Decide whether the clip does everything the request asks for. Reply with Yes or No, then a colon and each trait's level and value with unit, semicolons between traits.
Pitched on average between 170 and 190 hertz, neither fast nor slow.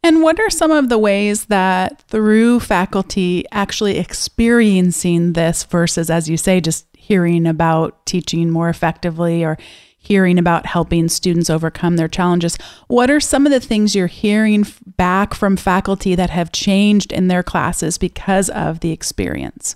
Yes: medium, 185 Hz; average, 160 wpm